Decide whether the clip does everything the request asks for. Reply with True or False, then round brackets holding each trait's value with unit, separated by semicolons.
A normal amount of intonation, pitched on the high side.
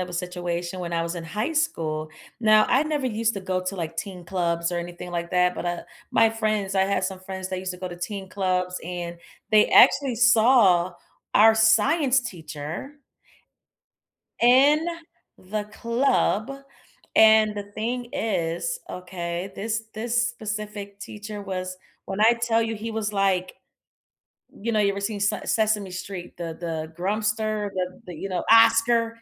True (3.8 semitones; 200 Hz)